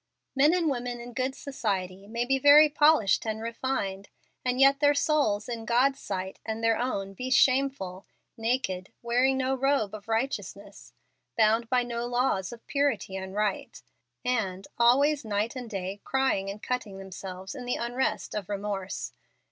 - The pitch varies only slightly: No, average, 4.9 semitones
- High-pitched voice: Yes, high, 235 Hz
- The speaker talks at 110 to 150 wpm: No, average, 160 wpm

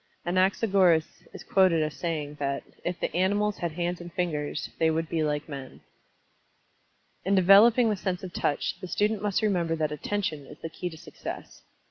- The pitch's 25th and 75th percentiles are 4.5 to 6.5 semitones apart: No, average, 3.6 semitones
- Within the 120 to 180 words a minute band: Yes, average, 175 wpm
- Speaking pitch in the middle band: Yes, medium, 175 Hz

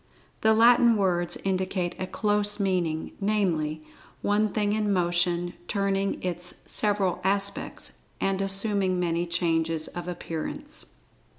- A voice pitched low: No, high, 190 Hz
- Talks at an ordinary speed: No, slow, 115 wpm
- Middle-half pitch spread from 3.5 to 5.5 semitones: No, average, 2.7 semitones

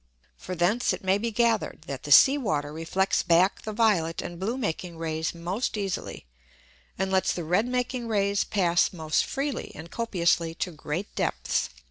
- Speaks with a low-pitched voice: No, high, 190 Hz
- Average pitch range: Yes, average, 4.9 semitones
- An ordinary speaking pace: Yes, average, 170 wpm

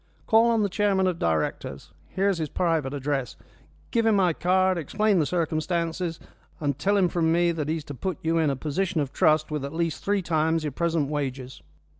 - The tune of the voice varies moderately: Yes, average, 3.9 semitones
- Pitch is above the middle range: No, medium, 165 Hz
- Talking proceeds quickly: Yes, fast, 210 wpm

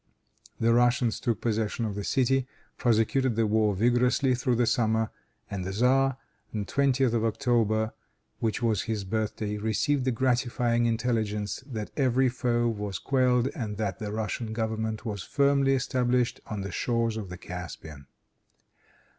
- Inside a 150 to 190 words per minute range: Yes, average, 155 wpm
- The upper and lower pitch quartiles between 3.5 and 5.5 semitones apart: No, average, 2.7 semitones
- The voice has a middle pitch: No, low, 115 Hz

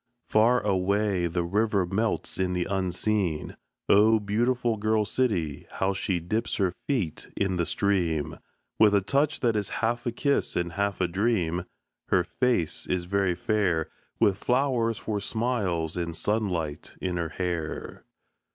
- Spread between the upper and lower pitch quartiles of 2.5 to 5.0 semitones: Yes, average, 4.0 semitones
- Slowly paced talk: No, average, 150 wpm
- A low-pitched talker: Yes, low, 100 Hz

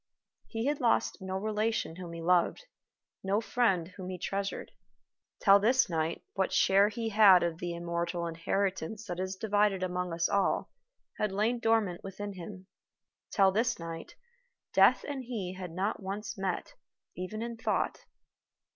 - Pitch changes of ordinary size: Yes, average, 3.3 semitones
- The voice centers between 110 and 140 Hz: No, high, 195 Hz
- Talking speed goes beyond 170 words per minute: No, average, 155 wpm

